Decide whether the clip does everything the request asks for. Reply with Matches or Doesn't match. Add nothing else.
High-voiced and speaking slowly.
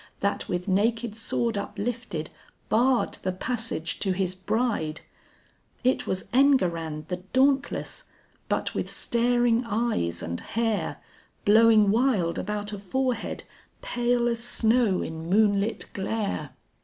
Matches